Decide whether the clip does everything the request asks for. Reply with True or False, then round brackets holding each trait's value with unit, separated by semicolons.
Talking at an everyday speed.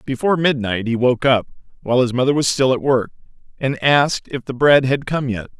False (215 wpm)